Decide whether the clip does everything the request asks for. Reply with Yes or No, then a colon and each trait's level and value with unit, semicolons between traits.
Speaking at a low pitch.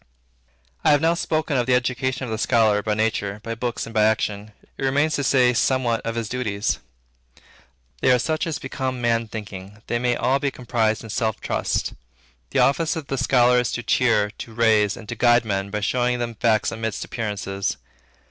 Yes: low, 120 Hz